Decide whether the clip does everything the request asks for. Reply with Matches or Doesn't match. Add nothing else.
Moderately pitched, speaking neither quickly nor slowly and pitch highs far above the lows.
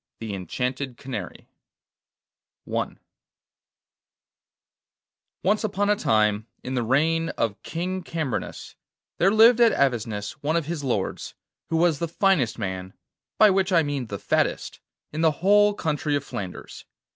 Doesn't match